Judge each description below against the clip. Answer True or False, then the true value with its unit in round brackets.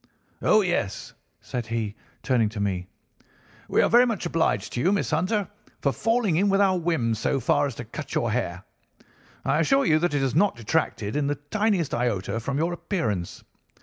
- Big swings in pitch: True (7.9 semitones)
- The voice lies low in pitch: False (145 Hz)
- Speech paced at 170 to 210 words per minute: True (190 wpm)